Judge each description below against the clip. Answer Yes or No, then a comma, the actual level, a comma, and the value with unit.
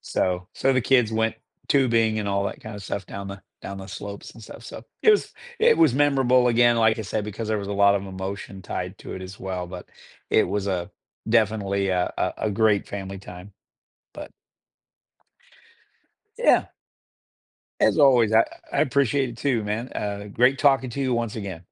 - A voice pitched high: No, low, 105 Hz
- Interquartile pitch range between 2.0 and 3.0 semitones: No, average, 3.6 semitones